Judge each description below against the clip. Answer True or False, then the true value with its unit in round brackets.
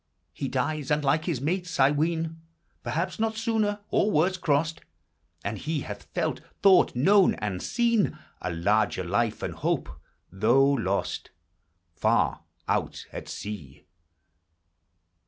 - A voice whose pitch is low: False (150 Hz)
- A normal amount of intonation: False (8.9 semitones)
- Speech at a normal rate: False (130 wpm)